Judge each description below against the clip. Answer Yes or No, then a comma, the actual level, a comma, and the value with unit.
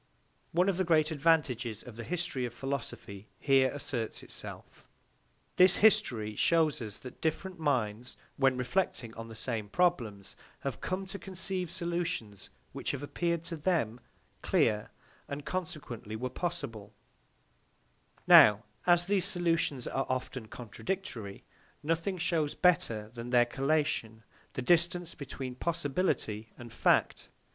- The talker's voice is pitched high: No, medium, 140 Hz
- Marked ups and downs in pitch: Yes, wide, 6.9 semitones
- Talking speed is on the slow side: Yes, slow, 130 wpm